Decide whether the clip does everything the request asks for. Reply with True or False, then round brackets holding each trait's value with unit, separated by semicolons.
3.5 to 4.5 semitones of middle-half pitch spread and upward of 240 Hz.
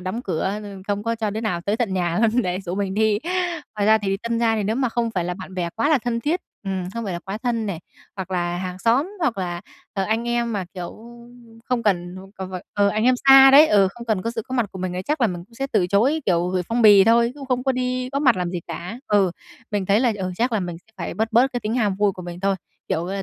False (4.1 semitones; 210 Hz)